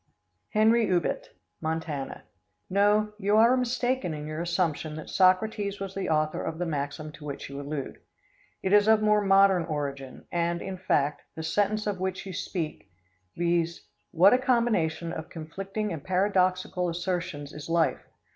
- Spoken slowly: No, average, 155 wpm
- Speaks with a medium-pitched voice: Yes, medium, 180 Hz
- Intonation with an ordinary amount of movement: Yes, average, 4.4 semitones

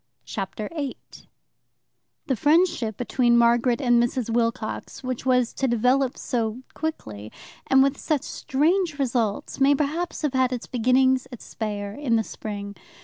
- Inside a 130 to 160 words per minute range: Yes, average, 145 wpm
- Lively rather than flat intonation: No, average, 3.1 semitones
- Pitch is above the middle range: Yes, very high, 250 Hz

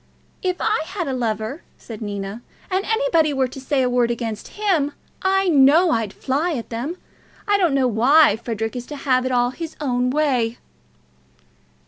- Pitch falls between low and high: No, very high, 265 Hz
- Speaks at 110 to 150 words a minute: No, average, 175 wpm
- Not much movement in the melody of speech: No, wide, 5.6 semitones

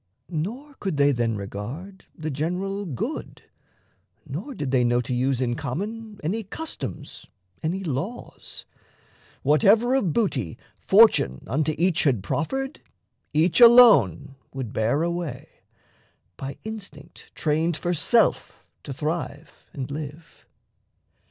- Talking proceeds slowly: Yes, slow, 120 wpm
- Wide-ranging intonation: Yes, wide, 6.9 semitones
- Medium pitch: Yes, medium, 155 Hz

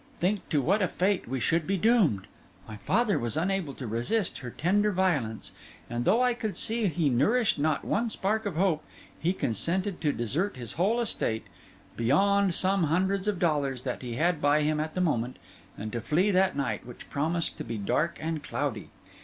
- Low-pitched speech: No, medium, 165 Hz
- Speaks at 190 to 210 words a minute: Yes, average, 195 wpm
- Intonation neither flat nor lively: No, wide, 6.7 semitones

